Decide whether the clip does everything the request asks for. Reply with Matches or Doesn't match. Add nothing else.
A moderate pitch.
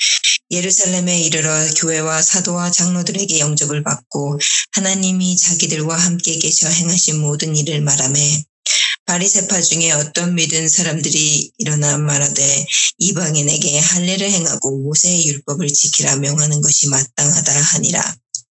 Matches